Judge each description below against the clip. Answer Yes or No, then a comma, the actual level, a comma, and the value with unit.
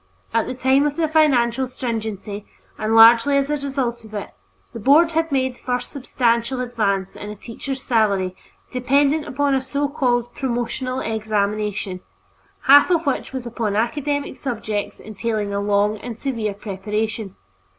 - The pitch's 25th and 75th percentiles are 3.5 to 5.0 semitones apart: Yes, average, 4.2 semitones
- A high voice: Yes, high, 240 Hz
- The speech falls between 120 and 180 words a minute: Yes, average, 155 wpm